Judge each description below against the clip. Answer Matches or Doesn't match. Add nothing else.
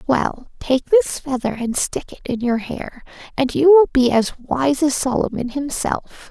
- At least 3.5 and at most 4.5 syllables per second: Matches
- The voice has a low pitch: Doesn't match